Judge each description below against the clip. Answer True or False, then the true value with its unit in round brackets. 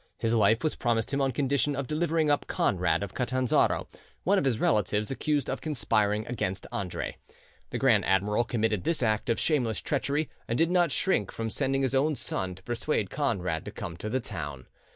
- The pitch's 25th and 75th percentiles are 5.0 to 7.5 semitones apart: True (5.3 semitones)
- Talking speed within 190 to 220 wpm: True (195 wpm)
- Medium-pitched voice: False (120 Hz)